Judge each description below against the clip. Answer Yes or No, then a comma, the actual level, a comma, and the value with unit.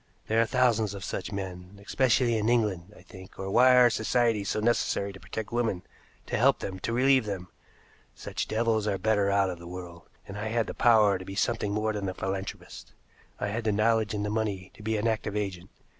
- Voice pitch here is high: No, low, 105 Hz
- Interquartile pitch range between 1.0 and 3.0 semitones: Yes, average, 2.7 semitones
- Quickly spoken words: Yes, fast, 220 wpm